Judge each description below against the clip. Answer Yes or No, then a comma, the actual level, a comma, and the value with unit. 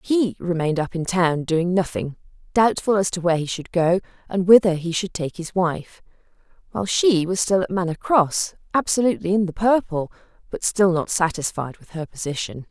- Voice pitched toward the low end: No, medium, 180 Hz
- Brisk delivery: No, average, 185 wpm